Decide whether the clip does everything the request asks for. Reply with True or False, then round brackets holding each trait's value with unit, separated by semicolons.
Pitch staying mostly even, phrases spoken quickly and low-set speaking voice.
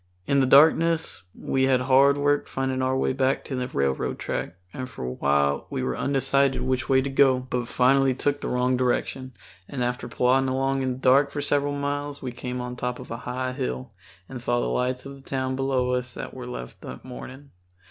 True (1.5 semitones; 210 wpm; 130 Hz)